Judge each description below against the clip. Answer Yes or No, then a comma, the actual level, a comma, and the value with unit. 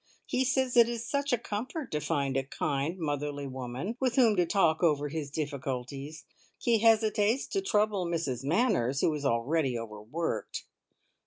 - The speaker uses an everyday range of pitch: No, wide, 8.2 semitones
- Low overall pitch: No, medium, 160 Hz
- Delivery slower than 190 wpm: Yes, average, 160 wpm